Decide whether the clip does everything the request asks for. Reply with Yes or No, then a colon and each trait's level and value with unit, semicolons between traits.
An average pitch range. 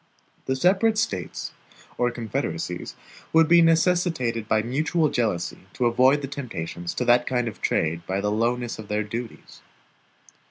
No: wide, 5.7 semitones